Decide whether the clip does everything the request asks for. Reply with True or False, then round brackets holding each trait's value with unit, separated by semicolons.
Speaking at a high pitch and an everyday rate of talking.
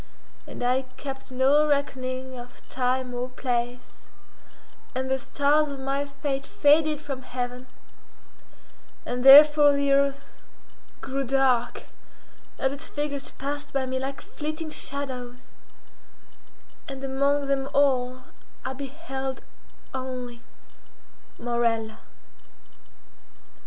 False (270 Hz; 100 wpm)